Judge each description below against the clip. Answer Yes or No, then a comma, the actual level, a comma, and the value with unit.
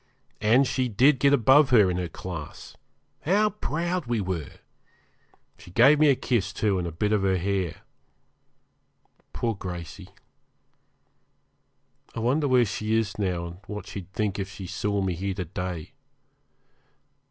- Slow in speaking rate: No, average, 155 wpm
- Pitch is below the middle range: Yes, low, 100 Hz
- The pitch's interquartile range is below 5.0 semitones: No, wide, 5.5 semitones